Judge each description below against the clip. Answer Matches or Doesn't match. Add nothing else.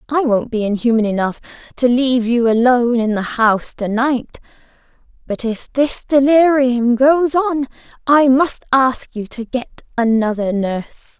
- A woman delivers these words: Matches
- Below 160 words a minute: Matches